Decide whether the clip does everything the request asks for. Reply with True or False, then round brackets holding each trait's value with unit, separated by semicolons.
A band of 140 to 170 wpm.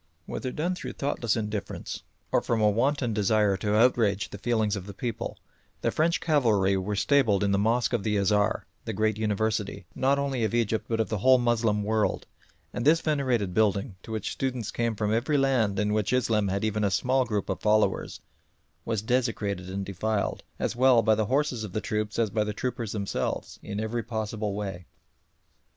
False (195 wpm)